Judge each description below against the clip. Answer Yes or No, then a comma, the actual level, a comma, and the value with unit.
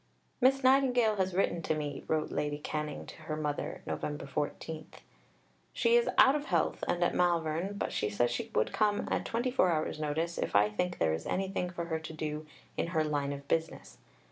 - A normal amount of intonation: Yes, average, 4.3 semitones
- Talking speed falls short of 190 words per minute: No, average, 195 wpm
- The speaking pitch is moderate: Yes, medium, 160 Hz